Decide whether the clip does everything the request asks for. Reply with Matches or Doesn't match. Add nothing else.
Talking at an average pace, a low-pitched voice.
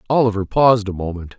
Matches